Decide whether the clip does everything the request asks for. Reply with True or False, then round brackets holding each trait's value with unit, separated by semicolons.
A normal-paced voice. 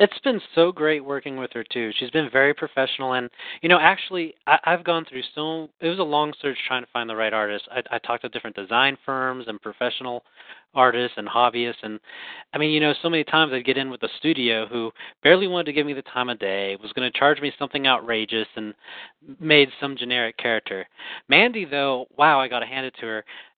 False (225 wpm)